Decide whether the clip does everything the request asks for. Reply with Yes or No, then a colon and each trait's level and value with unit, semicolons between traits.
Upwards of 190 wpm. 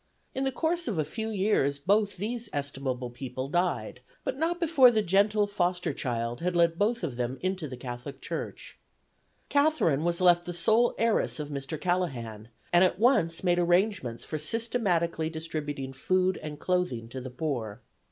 No: average, 170 wpm